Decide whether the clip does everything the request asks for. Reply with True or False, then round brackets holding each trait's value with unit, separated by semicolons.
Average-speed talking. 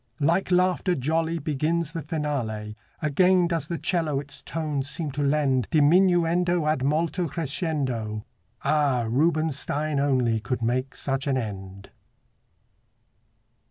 False (120 wpm)